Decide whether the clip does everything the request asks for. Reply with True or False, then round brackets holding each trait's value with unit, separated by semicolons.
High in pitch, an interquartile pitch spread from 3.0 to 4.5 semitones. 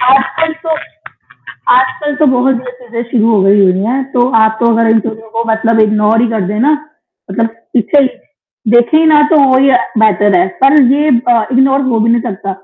True (235 Hz; 3.5 semitones)